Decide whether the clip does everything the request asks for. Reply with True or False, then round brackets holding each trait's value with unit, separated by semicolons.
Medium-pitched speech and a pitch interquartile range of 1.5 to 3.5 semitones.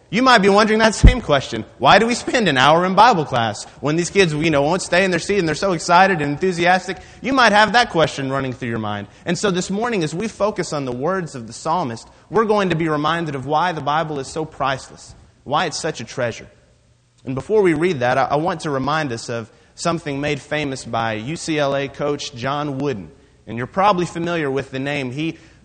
False (155 Hz; 5.5 semitones)